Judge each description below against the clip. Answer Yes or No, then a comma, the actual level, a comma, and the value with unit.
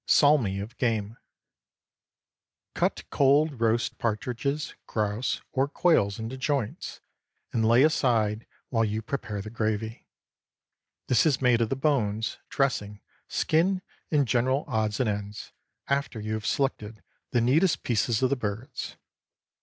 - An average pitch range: Yes, average, 4.3 semitones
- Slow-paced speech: Yes, slow, 130 wpm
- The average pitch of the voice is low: Yes, low, 115 Hz